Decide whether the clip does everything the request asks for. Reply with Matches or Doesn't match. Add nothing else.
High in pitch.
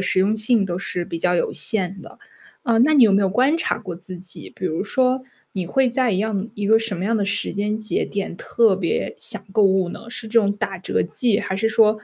Matches